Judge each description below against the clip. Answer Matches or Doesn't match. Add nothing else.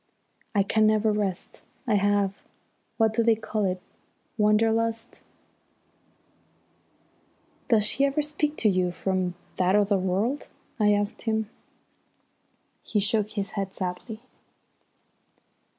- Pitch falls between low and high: Doesn't match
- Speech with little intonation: Matches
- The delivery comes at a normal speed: Doesn't match